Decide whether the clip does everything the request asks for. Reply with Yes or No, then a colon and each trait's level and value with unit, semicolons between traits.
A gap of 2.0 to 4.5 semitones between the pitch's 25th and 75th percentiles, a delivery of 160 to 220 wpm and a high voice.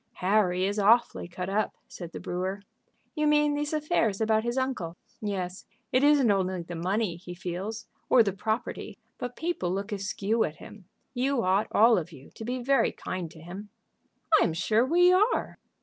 No: average, 5.3 semitones; average, 180 wpm; high, 210 Hz